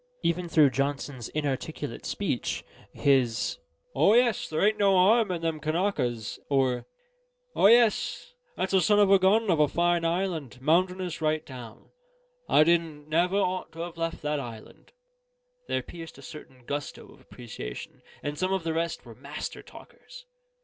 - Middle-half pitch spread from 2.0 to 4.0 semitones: No, average, 4.7 semitones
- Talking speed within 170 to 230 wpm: No, average, 160 wpm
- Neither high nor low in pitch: Yes, medium, 165 Hz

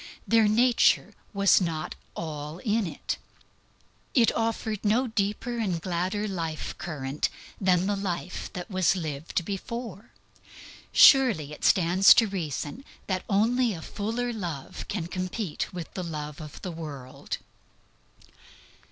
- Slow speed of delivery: Yes, slow, 125 wpm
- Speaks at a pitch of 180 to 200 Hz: Yes, medium, 185 Hz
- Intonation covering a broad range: No, average, 4.8 semitones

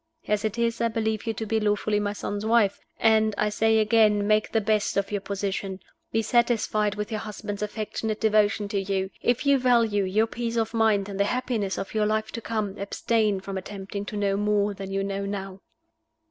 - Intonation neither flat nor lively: No, narrow, 1.7 semitones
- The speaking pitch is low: No, high, 210 Hz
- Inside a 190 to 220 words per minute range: Yes, fast, 205 wpm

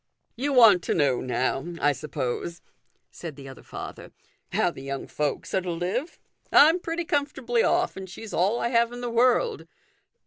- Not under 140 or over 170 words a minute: No, average, 185 wpm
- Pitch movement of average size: No, wide, 8.8 semitones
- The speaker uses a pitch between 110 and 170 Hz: No, high, 200 Hz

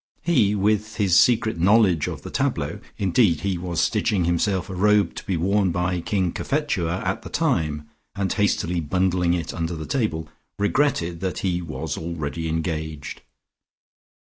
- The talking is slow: No, average, 150 wpm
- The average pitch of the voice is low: Yes, very low, 90 Hz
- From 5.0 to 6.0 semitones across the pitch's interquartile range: No, average, 3.6 semitones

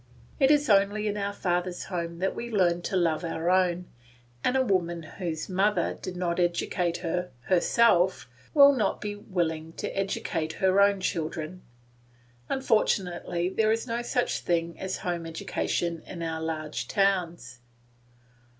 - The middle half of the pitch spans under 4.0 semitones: Yes, average, 3.0 semitones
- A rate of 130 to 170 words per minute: Yes, average, 150 wpm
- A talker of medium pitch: Yes, medium, 180 Hz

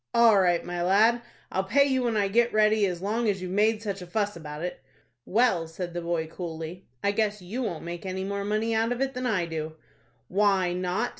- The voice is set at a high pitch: Yes, high, 195 Hz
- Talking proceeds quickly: Yes, fast, 220 wpm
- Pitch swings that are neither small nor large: Yes, average, 3.9 semitones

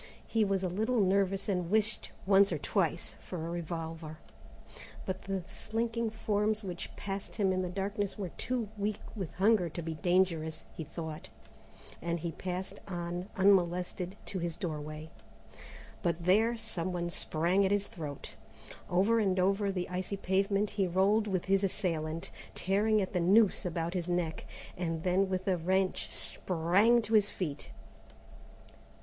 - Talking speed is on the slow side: No, average, 155 wpm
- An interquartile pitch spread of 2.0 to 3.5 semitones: Yes, average, 2.7 semitones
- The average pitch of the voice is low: No, medium, 185 Hz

